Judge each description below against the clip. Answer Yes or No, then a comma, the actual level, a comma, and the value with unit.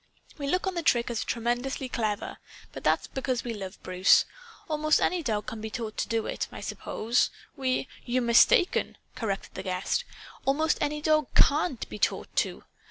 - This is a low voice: No, high, 245 Hz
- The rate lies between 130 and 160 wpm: No, average, 180 wpm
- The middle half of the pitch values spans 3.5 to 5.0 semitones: No, wide, 5.4 semitones